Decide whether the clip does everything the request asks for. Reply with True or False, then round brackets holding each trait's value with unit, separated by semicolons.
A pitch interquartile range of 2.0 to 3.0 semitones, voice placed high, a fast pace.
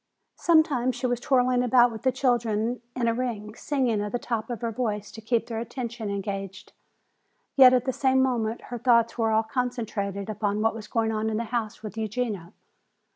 False (2.5 semitones; 230 Hz; 195 wpm)